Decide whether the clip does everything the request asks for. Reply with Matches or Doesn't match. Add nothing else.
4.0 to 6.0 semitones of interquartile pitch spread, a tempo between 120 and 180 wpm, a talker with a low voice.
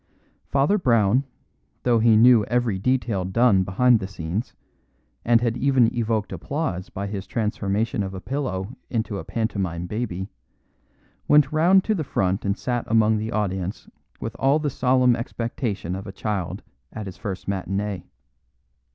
Matches